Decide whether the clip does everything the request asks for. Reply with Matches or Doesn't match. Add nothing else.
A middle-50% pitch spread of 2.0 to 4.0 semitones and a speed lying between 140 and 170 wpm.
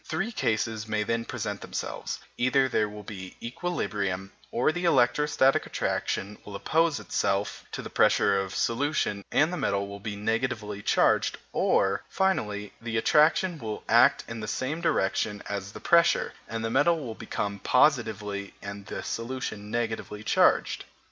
Doesn't match